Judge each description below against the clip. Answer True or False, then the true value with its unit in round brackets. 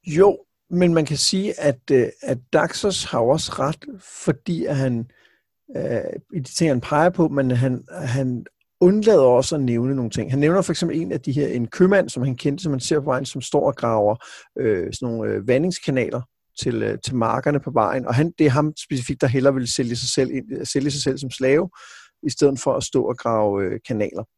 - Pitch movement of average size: True (3.5 semitones)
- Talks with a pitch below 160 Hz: True (140 Hz)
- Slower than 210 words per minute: False (215 wpm)